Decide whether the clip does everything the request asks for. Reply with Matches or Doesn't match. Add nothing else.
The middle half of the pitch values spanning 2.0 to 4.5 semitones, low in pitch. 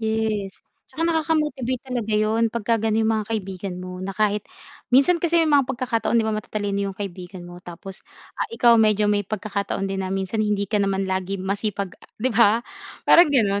Doesn't match